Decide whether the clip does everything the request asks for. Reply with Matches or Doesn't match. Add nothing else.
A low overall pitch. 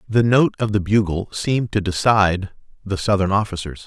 Matches